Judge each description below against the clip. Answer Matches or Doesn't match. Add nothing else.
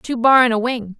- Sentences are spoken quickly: Matches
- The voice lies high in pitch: Matches